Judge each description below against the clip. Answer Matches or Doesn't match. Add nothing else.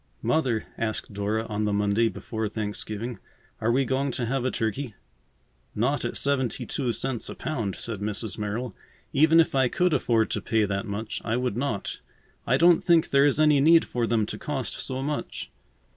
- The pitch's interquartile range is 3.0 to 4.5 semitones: Matches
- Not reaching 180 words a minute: Doesn't match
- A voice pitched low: Matches